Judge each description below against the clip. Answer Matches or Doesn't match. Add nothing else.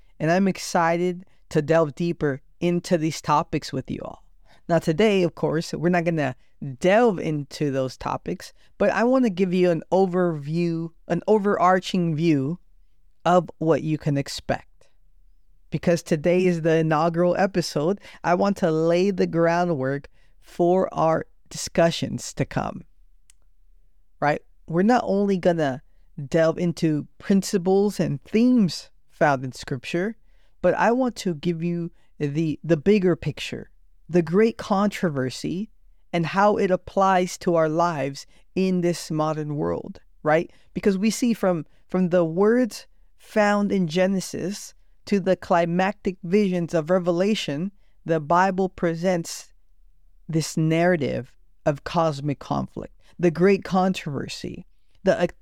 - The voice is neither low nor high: Matches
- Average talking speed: Doesn't match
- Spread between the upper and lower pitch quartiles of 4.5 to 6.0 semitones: Doesn't match